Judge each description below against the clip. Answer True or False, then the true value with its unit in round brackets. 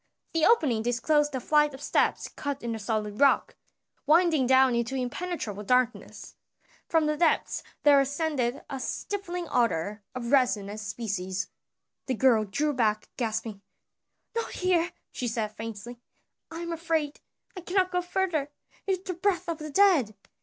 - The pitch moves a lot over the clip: True (6.4 semitones)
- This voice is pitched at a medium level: False (270 Hz)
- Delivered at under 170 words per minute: True (155 wpm)